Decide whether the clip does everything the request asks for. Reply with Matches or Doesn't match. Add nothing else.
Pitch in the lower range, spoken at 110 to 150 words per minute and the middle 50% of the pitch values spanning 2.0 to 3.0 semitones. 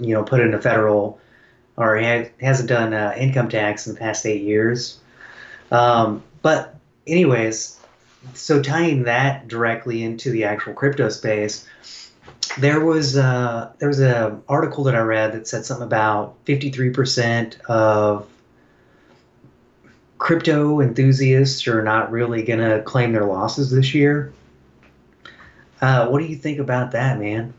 Doesn't match